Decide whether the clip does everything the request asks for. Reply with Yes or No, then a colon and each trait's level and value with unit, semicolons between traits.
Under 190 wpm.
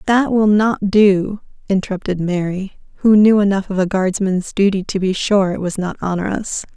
Yes: average, 180 wpm